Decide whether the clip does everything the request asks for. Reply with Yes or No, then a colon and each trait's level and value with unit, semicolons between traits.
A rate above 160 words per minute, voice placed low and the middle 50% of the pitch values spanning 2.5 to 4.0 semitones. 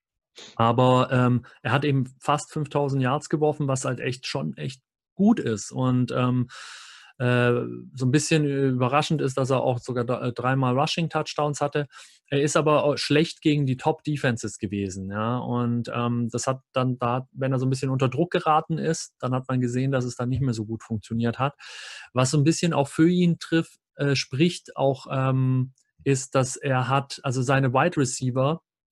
Yes: fast, 190 wpm; low, 130 Hz; average, 3.0 semitones